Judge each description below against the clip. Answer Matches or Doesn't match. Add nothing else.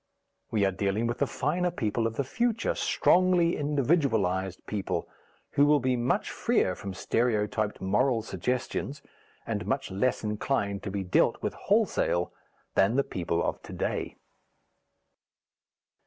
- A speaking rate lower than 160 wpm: Matches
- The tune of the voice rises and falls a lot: Matches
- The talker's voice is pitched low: Matches